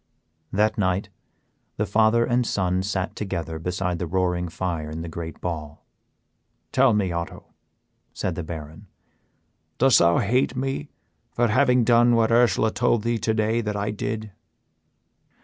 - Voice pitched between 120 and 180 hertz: No, low, 105 Hz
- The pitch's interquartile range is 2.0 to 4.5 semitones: No, average, 5.0 semitones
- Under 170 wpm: Yes, average, 145 wpm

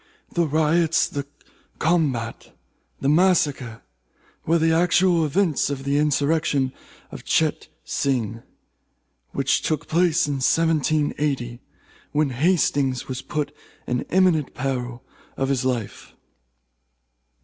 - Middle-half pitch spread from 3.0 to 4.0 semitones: Yes, average, 3.7 semitones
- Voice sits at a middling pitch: Yes, medium, 145 Hz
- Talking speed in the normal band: No, slow, 105 wpm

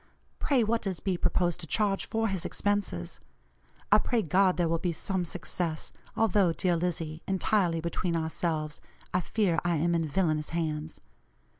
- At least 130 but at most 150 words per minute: No, average, 160 wpm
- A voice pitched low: No, medium, 175 Hz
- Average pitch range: Yes, average, 3.1 semitones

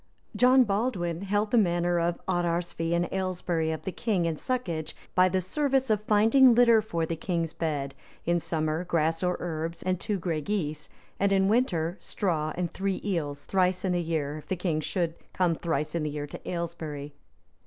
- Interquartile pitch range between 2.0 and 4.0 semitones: Yes, average, 3.3 semitones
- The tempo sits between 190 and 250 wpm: Yes, average, 195 wpm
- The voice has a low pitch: No, medium, 175 Hz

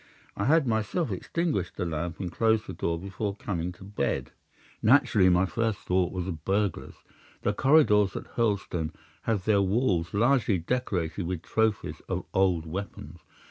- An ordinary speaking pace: Yes, average, 155 wpm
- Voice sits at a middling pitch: No, low, 100 Hz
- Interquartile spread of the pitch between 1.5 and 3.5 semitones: No, average, 3.9 semitones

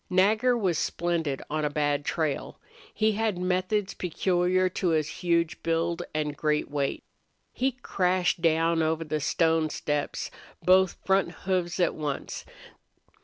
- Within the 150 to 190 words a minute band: No, slow, 135 wpm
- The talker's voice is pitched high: No, medium, 170 Hz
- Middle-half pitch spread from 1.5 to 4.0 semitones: Yes, average, 3.2 semitones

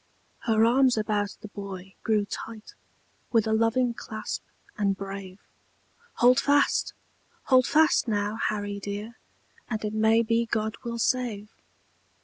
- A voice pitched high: Yes, high, 220 Hz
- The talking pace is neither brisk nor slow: No, slow, 130 wpm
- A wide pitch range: No, narrow, 2.4 semitones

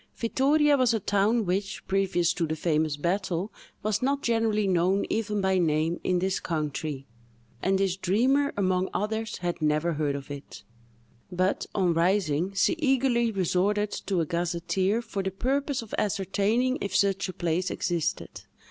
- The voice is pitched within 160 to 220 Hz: Yes, high, 190 Hz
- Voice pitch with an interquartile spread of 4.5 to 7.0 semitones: No, average, 3.9 semitones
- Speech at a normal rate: Yes, average, 155 wpm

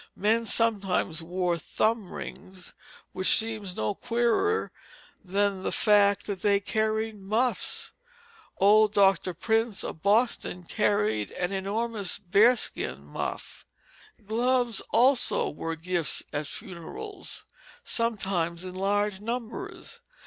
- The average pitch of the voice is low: No, high, 205 Hz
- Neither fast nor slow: No, slow, 105 wpm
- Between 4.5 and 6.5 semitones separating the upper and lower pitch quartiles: No, average, 3.5 semitones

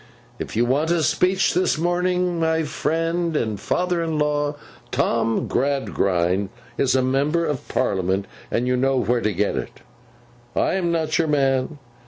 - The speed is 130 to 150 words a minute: No, average, 160 wpm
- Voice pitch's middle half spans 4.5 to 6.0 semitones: Yes, wide, 5.6 semitones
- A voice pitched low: No, medium, 145 Hz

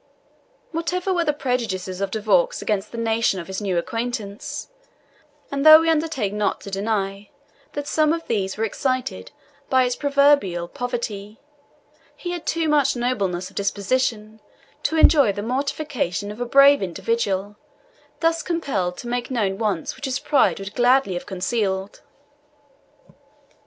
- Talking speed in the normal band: Yes, average, 150 wpm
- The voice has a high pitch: Yes, high, 230 Hz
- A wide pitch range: Yes, wide, 5.9 semitones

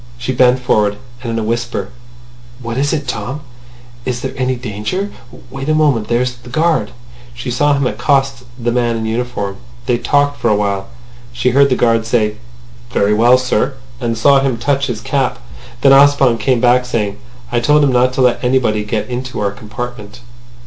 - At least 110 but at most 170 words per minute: No, average, 185 wpm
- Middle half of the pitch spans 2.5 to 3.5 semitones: Yes, average, 2.9 semitones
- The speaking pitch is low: Yes, low, 125 Hz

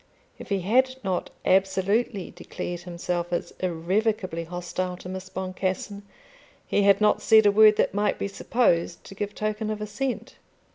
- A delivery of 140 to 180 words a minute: Yes, average, 155 wpm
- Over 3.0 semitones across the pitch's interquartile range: No, average, 2.7 semitones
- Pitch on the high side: Yes, high, 195 Hz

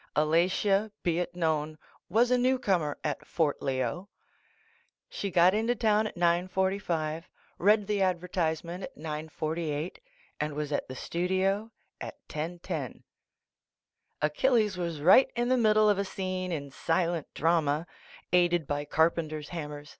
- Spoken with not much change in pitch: No, average, 4.1 semitones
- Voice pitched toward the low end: No, medium, 175 Hz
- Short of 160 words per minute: Yes, average, 140 wpm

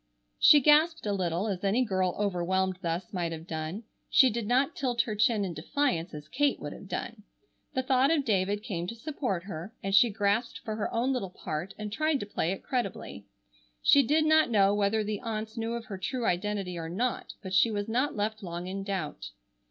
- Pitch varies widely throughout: No, average, 4.5 semitones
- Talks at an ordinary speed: No, fast, 210 wpm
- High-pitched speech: Yes, high, 205 Hz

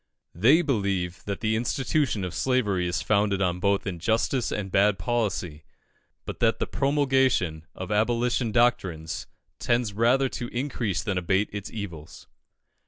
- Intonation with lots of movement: No, average, 4.7 semitones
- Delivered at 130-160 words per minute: Yes, average, 140 wpm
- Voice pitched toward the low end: Yes, low, 105 Hz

